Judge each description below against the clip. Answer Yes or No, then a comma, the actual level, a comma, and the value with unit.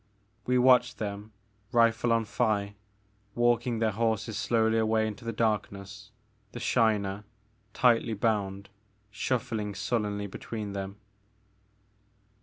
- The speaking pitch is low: Yes, low, 110 Hz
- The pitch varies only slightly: Yes, narrow, 2.3 semitones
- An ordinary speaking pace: No, slow, 105 wpm